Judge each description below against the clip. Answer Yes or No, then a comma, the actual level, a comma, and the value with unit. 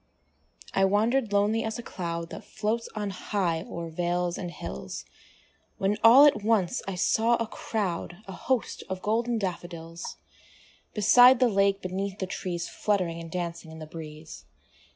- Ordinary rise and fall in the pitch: Yes, average, 4.4 semitones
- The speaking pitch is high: Yes, high, 195 Hz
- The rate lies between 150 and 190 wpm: Yes, average, 155 wpm